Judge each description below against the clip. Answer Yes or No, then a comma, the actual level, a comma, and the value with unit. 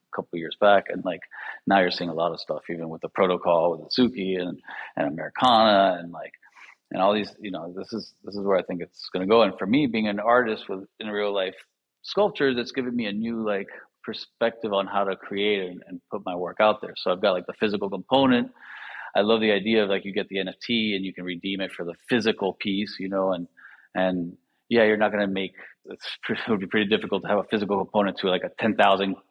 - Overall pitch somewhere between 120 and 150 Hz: No, low, 100 Hz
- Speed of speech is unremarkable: No, fast, 250 wpm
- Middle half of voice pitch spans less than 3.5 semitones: Yes, narrow, 2.5 semitones